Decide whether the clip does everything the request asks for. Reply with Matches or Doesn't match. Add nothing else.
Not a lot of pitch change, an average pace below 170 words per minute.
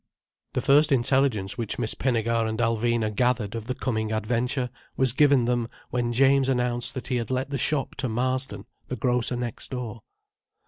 Doesn't match